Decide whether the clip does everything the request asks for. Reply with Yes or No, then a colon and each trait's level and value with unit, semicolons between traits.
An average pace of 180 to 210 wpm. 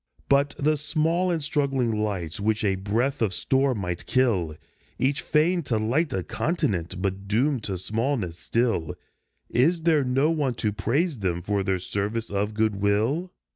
No: average, 165 wpm